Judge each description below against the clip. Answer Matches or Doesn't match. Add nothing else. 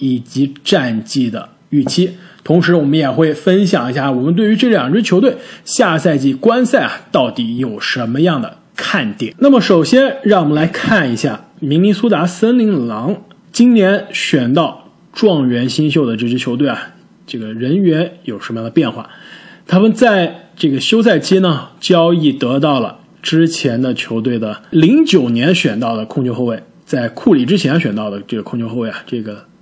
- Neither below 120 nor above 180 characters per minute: Doesn't match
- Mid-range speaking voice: Matches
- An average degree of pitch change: Doesn't match